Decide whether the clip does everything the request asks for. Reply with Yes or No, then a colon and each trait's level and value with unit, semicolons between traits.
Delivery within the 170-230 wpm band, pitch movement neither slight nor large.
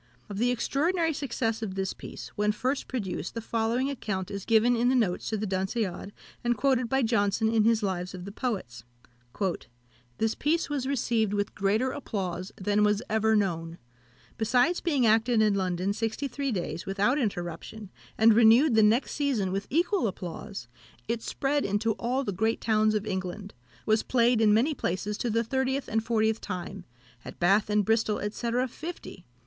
Yes: average, 175 wpm; average, 3.7 semitones